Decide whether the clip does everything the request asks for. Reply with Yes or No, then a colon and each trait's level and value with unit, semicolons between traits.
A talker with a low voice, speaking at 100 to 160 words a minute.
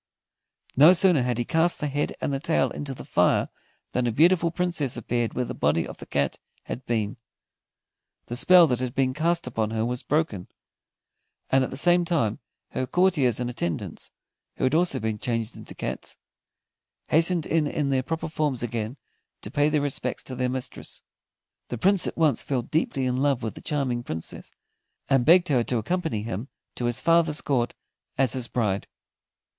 No: low, 130 Hz; average, 185 wpm